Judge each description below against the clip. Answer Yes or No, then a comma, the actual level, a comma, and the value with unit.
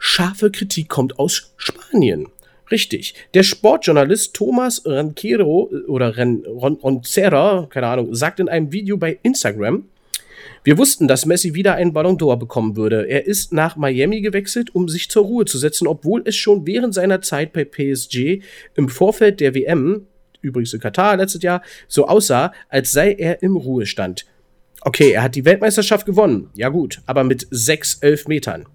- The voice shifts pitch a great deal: Yes, wide, 6.7 semitones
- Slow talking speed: No, average, 165 wpm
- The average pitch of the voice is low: No, medium, 165 Hz